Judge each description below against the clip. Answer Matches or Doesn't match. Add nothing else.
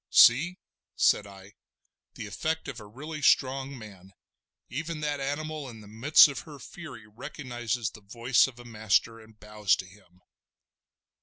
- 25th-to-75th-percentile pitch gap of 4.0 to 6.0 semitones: Matches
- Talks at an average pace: Matches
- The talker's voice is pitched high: Doesn't match